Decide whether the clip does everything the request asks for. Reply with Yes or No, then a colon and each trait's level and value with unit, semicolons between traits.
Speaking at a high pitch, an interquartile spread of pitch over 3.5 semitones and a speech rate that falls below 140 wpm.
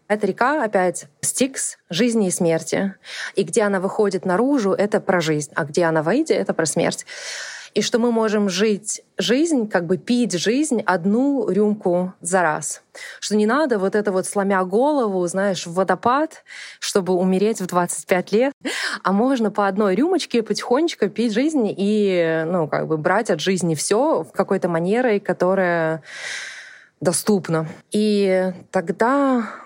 No: high, 200 Hz; average, 4.1 semitones; average, 150 wpm